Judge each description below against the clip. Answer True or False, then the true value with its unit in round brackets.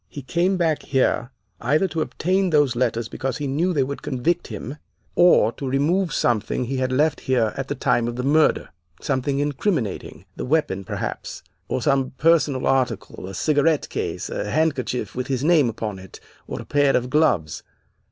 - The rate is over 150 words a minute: True (180 wpm)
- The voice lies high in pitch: False (135 Hz)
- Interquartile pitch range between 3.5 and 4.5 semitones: True (4.0 semitones)